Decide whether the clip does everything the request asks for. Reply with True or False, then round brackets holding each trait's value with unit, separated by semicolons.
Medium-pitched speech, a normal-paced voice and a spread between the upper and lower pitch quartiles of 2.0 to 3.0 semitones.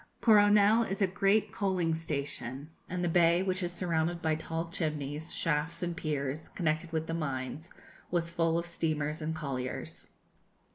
True (165 Hz; 155 wpm; 2.5 semitones)